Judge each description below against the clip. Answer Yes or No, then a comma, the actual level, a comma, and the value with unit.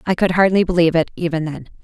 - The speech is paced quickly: Yes, fast, 230 wpm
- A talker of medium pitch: Yes, medium, 170 Hz